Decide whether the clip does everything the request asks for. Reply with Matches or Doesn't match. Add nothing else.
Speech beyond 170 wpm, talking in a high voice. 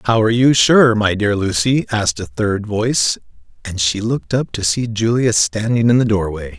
Doesn't match